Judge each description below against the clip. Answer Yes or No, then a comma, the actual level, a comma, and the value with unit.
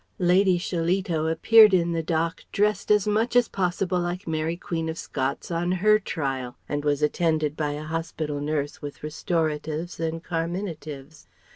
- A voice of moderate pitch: Yes, medium, 165 Hz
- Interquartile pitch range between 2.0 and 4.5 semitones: Yes, average, 2.9 semitones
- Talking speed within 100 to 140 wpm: No, average, 155 wpm